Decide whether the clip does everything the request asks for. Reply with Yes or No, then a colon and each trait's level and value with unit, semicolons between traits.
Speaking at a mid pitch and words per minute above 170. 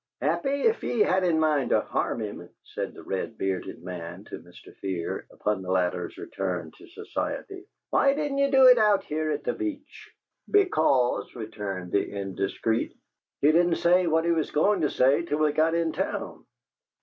Yes: medium, 155 Hz; average, 185 wpm